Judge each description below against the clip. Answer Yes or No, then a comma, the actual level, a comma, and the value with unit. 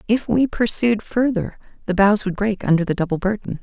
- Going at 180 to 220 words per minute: Yes, average, 200 wpm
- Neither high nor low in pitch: No, high, 205 Hz